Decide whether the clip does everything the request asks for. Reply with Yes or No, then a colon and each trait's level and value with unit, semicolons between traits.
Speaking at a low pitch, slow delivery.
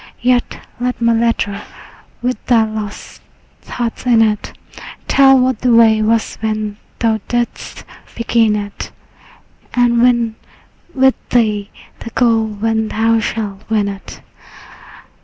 No: high, 225 Hz; slow, 120 wpm